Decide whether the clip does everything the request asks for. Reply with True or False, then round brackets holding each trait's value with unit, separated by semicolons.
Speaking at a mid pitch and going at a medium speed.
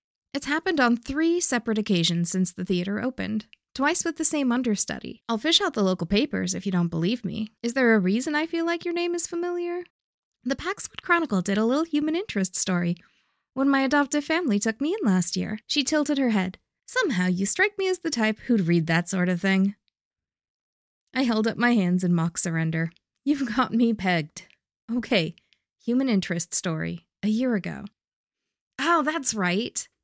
False (230 Hz; 190 wpm)